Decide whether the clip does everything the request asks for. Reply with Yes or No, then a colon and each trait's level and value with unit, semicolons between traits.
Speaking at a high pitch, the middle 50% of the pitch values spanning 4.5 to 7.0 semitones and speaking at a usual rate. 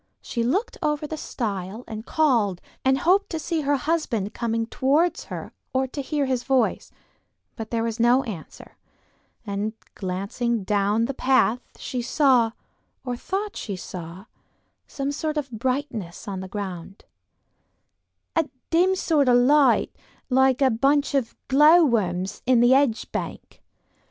Yes: very high, 250 Hz; average, 4.9 semitones; average, 145 wpm